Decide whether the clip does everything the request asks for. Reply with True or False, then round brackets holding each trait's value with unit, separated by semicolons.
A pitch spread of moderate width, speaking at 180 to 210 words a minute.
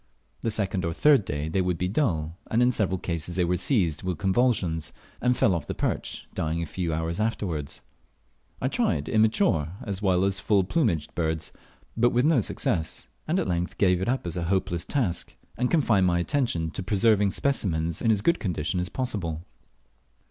True (5.0 semitones; 195 wpm)